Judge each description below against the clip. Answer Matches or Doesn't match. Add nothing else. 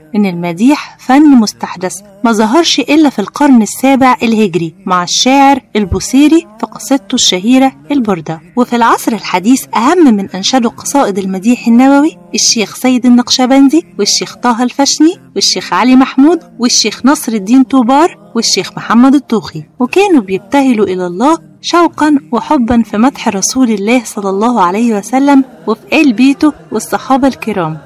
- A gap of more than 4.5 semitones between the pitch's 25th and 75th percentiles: Matches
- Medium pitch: Doesn't match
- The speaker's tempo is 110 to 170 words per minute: Matches